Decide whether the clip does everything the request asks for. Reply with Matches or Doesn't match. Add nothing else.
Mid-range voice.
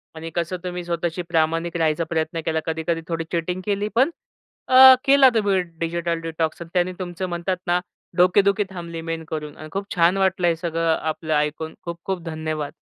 Matches